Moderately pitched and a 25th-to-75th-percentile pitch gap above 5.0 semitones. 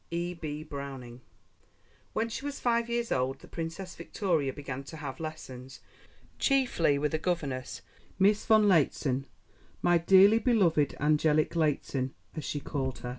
Yes: medium, 155 Hz; wide, 5.6 semitones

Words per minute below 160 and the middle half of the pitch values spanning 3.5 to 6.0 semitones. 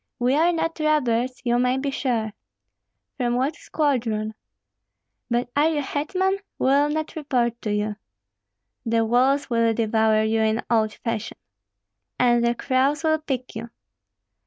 Yes: average, 145 wpm; average, 4.1 semitones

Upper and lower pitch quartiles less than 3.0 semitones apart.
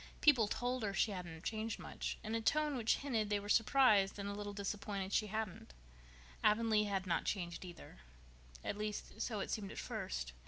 Yes: narrow, 2.4 semitones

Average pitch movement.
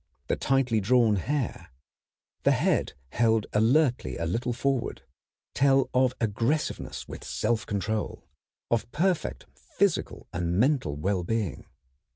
Yes: average, 4.5 semitones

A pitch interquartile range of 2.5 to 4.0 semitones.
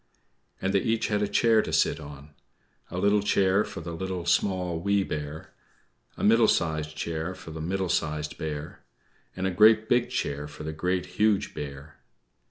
No: average, 4.6 semitones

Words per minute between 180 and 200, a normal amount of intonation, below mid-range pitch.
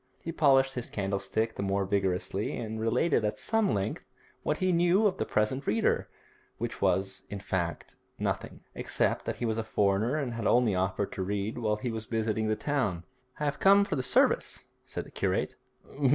Yes: average, 190 wpm; average, 5.0 semitones; low, 110 Hz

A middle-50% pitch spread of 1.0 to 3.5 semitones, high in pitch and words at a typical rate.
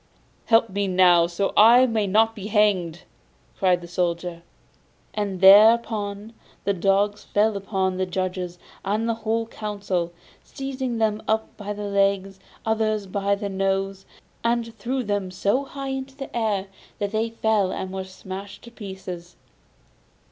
Yes: average, 2.7 semitones; high, 200 Hz; average, 150 wpm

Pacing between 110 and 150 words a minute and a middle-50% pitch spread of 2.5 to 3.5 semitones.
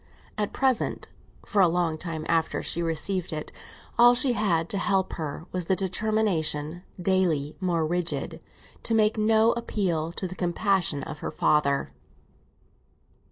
No: average, 145 wpm; average, 4.5 semitones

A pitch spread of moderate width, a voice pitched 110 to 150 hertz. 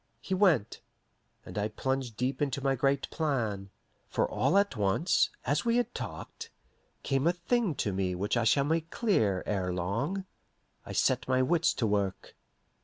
No: wide, 8.3 semitones; low, 135 Hz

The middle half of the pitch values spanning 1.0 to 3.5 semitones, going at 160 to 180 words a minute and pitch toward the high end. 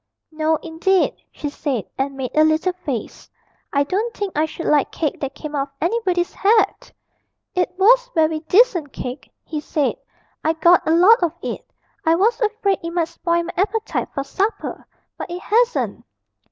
No: average, 4.3 semitones; average, 175 wpm; very high, 335 Hz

